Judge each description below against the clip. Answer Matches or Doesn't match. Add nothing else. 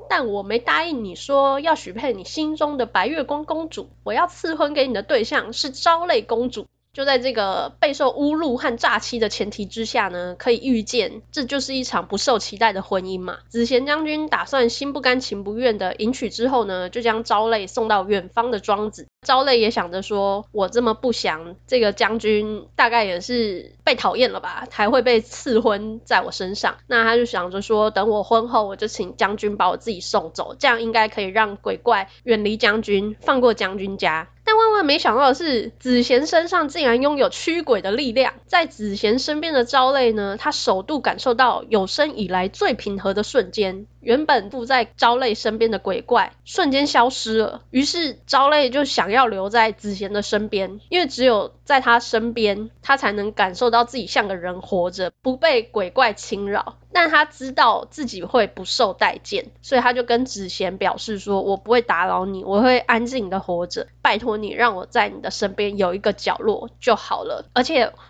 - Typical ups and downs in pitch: Matches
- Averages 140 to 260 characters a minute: Doesn't match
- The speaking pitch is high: Matches